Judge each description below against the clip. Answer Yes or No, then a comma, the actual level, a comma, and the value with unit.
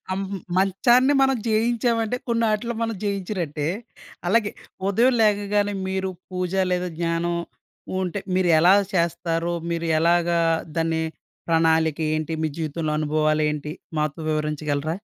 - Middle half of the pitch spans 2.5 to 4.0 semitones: No, average, 4.4 semitones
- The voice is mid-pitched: Yes, medium, 175 Hz